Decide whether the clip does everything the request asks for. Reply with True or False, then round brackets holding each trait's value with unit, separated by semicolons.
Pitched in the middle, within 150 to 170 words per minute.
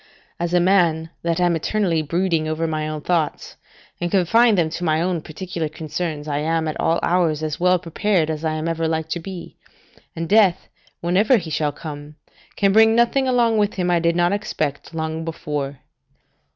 False (165 Hz; 190 wpm)